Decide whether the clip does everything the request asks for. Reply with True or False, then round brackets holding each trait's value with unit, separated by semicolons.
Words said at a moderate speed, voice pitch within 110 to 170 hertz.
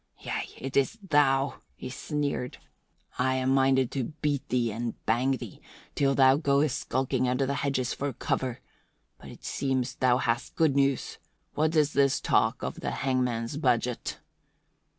True (155 wpm; 135 Hz)